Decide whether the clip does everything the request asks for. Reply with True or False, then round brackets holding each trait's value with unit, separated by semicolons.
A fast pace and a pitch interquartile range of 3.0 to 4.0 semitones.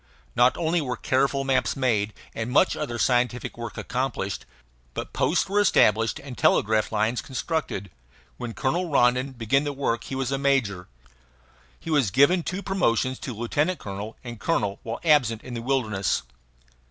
False (160 wpm; 3.7 semitones)